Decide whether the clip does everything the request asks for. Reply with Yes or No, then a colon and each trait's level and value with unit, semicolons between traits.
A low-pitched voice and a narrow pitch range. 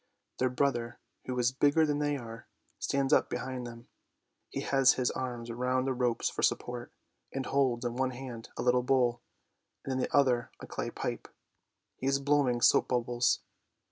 Yes: low, 125 Hz; narrow, 1.9 semitones